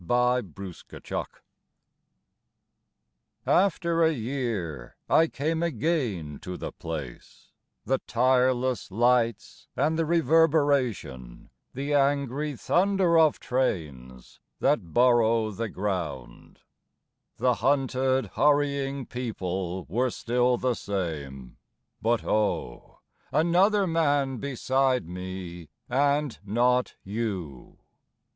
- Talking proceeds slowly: Yes, slow, 95 wpm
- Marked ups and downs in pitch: Yes, wide, 7.0 semitones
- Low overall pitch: Yes, low, 125 Hz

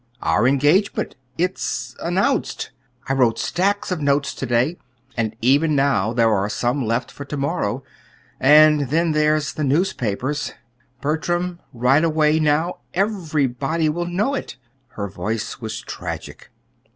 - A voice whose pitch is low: No, medium, 145 Hz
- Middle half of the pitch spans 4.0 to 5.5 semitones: Yes, average, 5.1 semitones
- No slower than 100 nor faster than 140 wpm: Yes, slow, 135 wpm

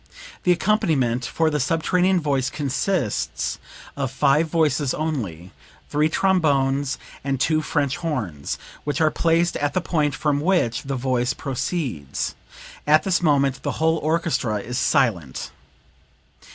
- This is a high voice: No, medium, 145 Hz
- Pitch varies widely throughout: No, average, 3.9 semitones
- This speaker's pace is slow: Yes, slow, 130 wpm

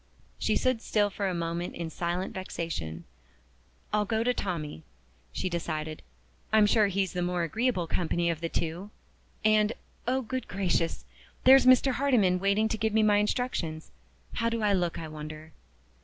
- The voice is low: No, high, 190 Hz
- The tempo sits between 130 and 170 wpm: Yes, average, 165 wpm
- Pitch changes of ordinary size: Yes, average, 4.7 semitones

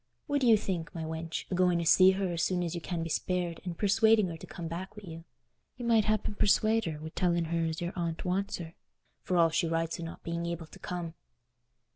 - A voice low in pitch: No, medium, 175 Hz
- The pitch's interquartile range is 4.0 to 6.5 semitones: No, narrow, 2.6 semitones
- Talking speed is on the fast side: Yes, fast, 245 wpm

